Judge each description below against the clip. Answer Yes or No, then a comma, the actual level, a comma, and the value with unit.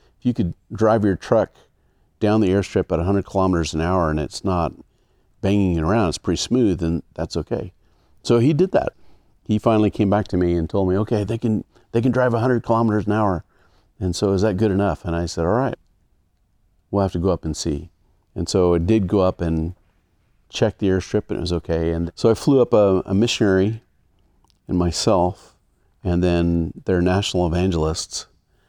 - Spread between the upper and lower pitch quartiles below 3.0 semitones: No, average, 3.7 semitones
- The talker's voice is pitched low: Yes, very low, 95 Hz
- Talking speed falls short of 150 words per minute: No, average, 200 wpm